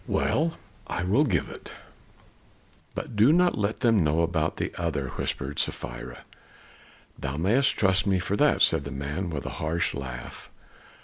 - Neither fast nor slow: Yes, average, 160 wpm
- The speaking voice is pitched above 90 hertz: No, very low, 85 Hz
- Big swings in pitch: Yes, wide, 6.5 semitones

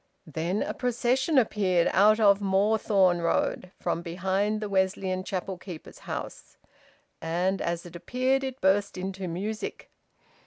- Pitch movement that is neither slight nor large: Yes, average, 3.0 semitones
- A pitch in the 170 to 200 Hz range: Yes, high, 190 Hz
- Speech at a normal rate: No, slow, 130 wpm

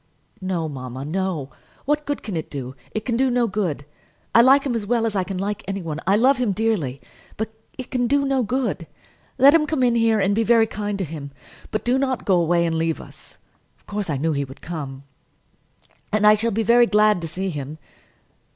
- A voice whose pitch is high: Yes, high, 205 Hz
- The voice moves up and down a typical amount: No, wide, 6.4 semitones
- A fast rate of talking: Yes, fast, 225 wpm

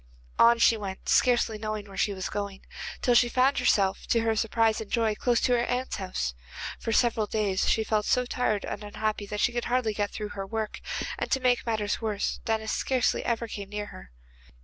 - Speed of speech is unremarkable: No, fast, 210 wpm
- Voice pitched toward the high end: Yes, high, 220 Hz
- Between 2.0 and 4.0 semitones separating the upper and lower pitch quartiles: Yes, narrow, 2.4 semitones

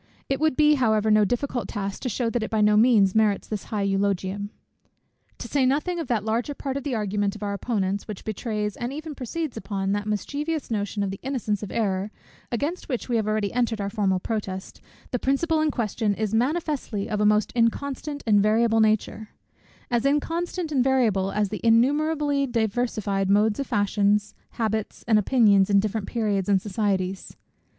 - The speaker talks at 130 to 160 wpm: No, average, 185 wpm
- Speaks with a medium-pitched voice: No, high, 220 Hz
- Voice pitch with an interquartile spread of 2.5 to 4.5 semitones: Yes, average, 4.2 semitones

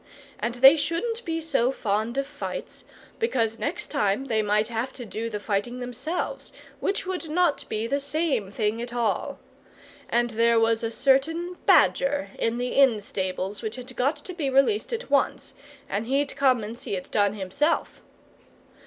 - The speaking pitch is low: No, high, 245 Hz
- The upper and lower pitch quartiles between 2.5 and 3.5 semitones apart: No, average, 4.7 semitones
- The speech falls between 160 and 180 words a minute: Yes, average, 170 wpm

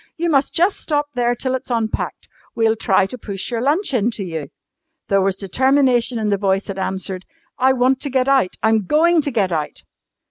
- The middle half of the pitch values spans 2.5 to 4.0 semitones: No, wide, 5.4 semitones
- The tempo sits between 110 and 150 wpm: No, fast, 205 wpm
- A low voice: No, high, 235 Hz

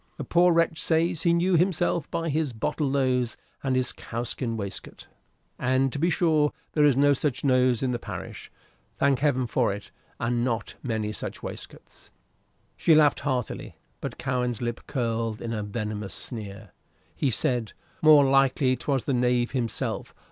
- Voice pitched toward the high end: No, low, 130 Hz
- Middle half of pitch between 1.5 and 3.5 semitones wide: No, average, 3.9 semitones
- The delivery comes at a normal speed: Yes, average, 160 wpm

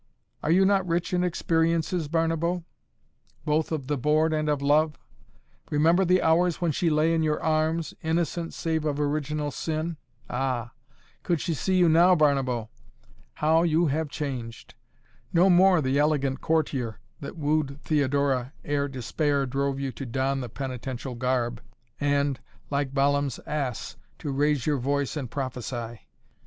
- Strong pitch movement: No, average, 3.1 semitones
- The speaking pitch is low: No, medium, 150 Hz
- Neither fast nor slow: Yes, average, 150 wpm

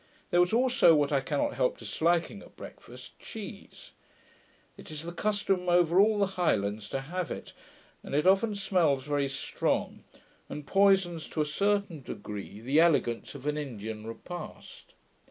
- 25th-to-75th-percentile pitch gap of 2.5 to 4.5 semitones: No, wide, 5.5 semitones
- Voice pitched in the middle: Yes, medium, 160 Hz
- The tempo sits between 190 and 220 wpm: No, average, 155 wpm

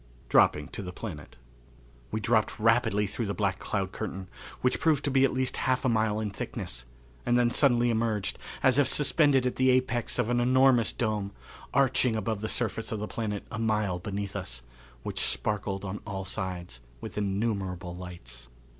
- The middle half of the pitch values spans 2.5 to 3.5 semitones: No, average, 4.0 semitones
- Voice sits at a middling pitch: No, low, 110 Hz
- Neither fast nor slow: Yes, average, 180 wpm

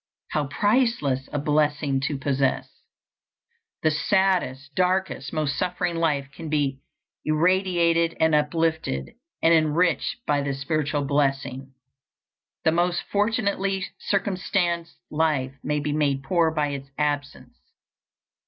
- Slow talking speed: Yes, slow, 115 wpm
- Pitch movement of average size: Yes, average, 3.6 semitones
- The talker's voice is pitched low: No, medium, 155 Hz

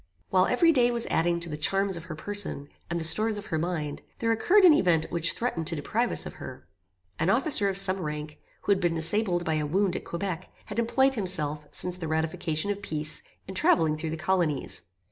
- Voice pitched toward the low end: No, medium, 180 Hz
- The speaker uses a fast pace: Yes, fast, 220 wpm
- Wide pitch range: No, average, 4.3 semitones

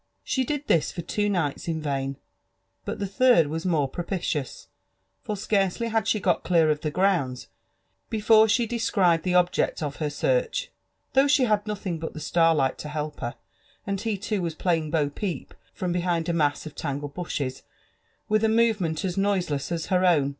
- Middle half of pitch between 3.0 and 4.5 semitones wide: No, average, 5.2 semitones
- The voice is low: No, medium, 175 Hz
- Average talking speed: Yes, average, 185 wpm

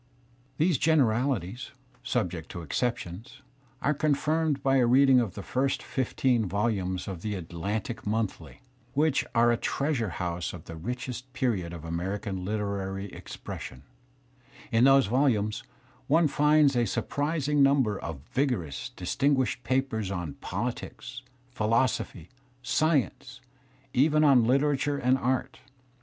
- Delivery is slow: Yes, slow, 125 wpm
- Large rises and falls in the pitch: Yes, wide, 5.8 semitones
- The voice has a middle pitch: No, low, 120 Hz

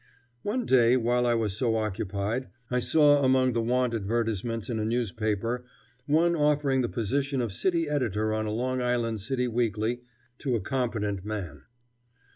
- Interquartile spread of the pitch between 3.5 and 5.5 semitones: No, average, 3.0 semitones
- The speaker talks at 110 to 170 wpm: Yes, average, 160 wpm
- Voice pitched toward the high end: No, low, 120 Hz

